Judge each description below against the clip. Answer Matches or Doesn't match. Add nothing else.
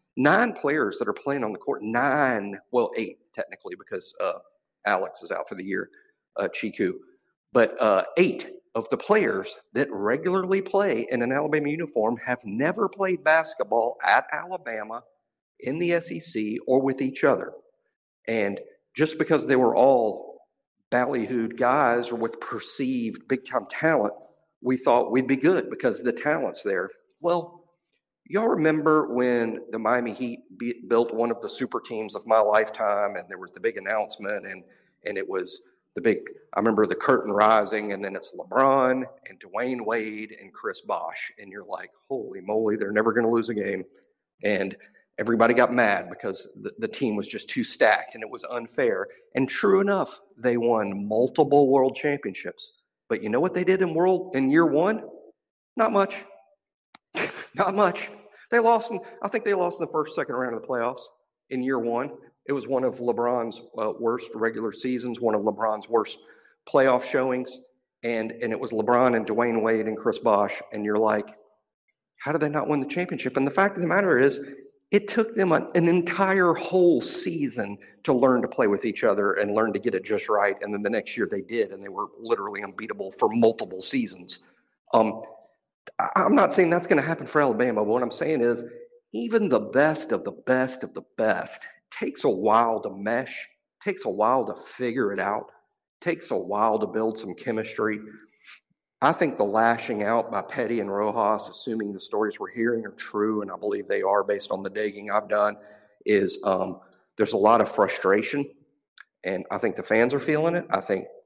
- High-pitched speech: Doesn't match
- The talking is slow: Doesn't match